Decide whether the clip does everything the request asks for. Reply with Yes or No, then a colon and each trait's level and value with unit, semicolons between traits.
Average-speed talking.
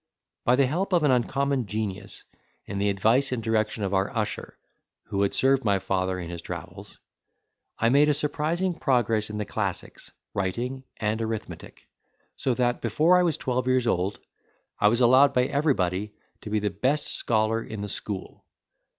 Yes: average, 175 wpm